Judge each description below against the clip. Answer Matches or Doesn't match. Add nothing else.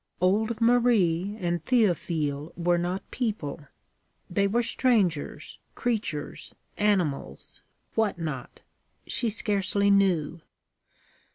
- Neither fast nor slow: Doesn't match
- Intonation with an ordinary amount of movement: Matches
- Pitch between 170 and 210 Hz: Matches